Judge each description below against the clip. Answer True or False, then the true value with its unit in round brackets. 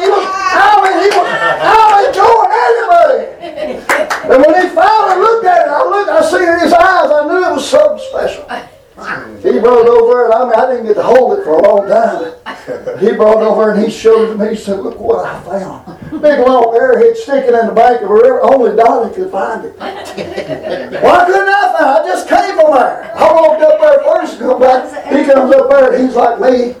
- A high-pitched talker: True (315 Hz)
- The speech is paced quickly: True (235 wpm)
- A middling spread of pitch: False (7.4 semitones)